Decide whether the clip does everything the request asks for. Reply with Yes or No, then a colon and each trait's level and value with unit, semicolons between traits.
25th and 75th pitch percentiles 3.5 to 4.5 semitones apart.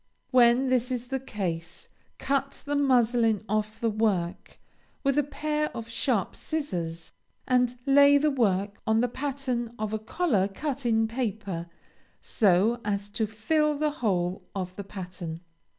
No: average, 5.2 semitones